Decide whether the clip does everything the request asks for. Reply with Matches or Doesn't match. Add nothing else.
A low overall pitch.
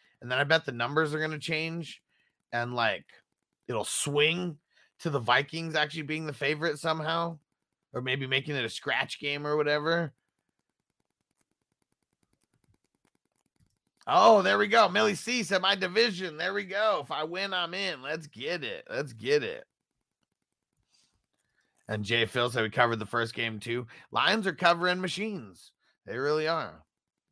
Doesn't match